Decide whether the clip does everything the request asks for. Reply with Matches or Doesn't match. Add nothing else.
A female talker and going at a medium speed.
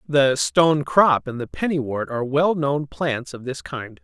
Doesn't match